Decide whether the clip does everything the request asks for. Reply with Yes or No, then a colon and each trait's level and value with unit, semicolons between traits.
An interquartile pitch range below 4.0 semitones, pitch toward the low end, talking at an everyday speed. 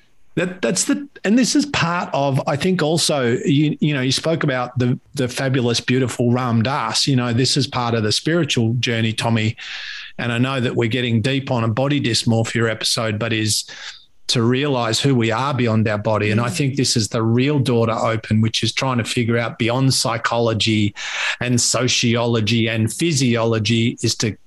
Yes: average, 2.8 semitones; low, 120 Hz; average, 195 wpm